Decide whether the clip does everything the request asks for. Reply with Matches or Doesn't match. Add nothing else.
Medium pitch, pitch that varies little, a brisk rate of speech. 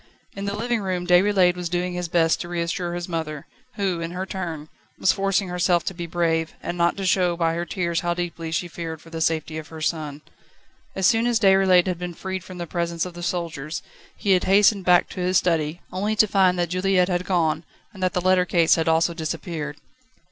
Matches